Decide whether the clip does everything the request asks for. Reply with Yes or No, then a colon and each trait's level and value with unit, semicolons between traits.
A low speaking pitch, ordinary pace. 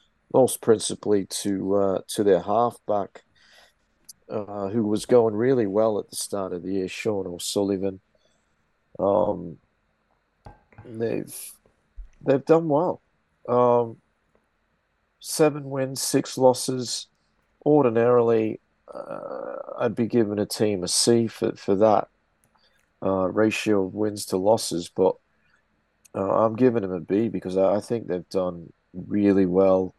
No: low, 105 Hz; slow, 130 wpm